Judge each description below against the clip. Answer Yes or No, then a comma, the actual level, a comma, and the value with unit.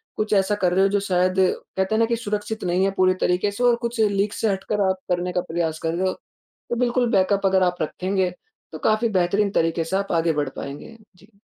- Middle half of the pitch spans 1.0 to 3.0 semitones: Yes, average, 2.7 semitones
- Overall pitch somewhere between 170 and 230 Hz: Yes, high, 190 Hz